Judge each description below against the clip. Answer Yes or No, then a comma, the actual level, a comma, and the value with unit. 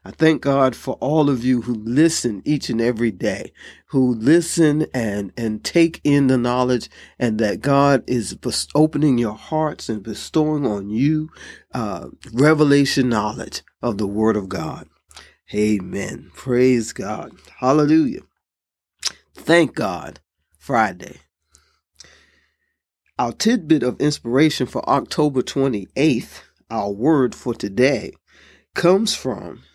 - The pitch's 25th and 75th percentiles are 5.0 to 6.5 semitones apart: Yes, wide, 5.6 semitones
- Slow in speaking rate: Yes, slow, 120 wpm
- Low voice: Yes, low, 130 Hz